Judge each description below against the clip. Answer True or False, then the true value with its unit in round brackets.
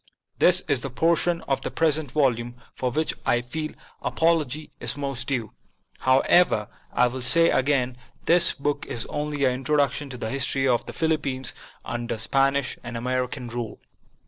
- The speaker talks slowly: False (160 wpm)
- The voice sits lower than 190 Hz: True (135 Hz)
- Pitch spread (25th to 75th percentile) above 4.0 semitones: False (3.4 semitones)